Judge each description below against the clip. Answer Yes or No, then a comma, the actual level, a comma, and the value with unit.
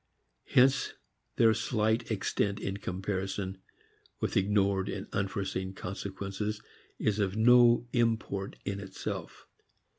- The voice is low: Yes, low, 100 Hz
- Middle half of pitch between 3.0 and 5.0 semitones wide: No, narrow, 2.4 semitones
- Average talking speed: No, slow, 100 wpm